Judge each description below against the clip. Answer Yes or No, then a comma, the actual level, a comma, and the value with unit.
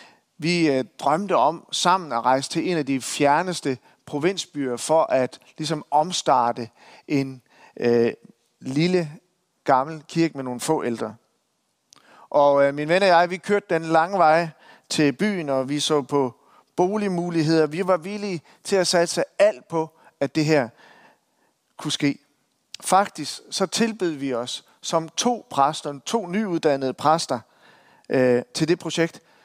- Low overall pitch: No, medium, 155 Hz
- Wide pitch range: No, average, 4.3 semitones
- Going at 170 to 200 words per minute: No, slow, 145 wpm